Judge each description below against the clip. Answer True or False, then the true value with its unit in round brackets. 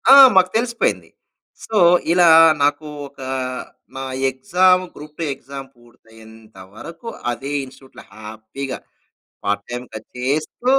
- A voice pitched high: False (135 Hz)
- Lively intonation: True (6.8 semitones)